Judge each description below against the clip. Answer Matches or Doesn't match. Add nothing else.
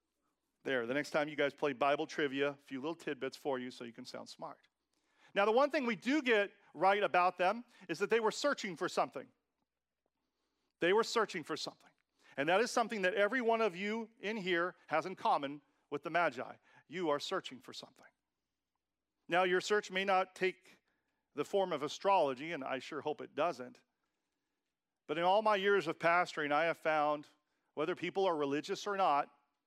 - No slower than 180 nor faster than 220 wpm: Matches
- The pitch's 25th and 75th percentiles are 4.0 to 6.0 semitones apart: Matches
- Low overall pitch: Doesn't match